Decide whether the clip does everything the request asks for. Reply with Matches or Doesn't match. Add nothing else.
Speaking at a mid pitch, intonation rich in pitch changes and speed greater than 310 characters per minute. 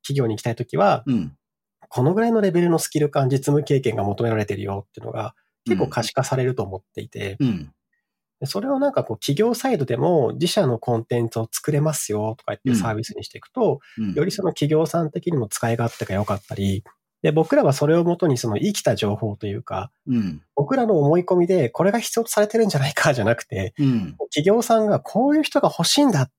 Matches